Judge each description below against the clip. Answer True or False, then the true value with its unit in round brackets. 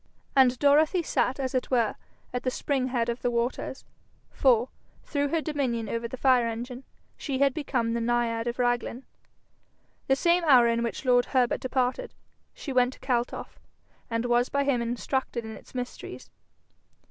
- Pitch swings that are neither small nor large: False (2.2 semitones)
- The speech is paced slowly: False (170 wpm)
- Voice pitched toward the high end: True (250 Hz)